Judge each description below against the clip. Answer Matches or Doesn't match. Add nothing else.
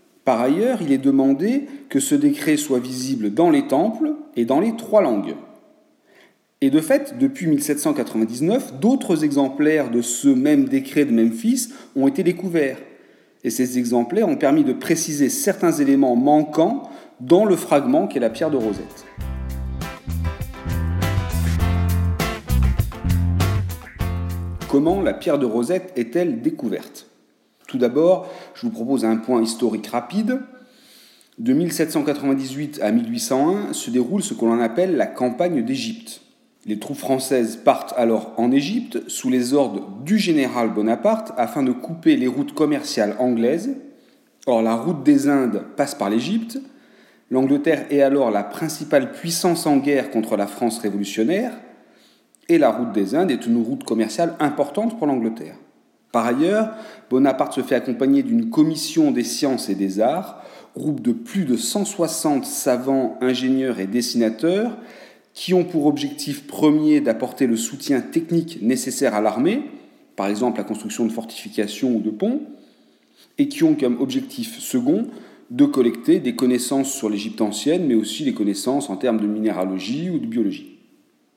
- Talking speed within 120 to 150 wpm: Matches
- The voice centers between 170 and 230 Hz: Doesn't match